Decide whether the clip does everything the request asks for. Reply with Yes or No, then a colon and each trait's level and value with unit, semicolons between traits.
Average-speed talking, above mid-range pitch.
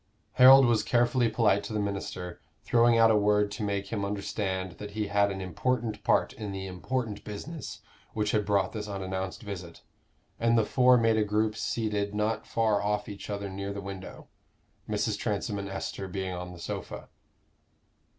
No: average, 180 wpm; low, 105 Hz